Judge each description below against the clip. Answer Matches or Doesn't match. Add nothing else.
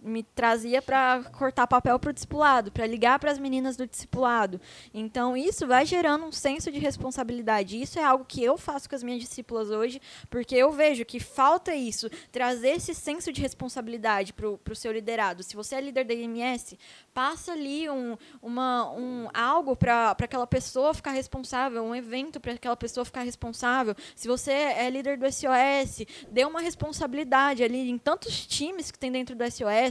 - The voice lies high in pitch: Matches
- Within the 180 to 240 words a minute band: Matches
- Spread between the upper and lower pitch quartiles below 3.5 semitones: Matches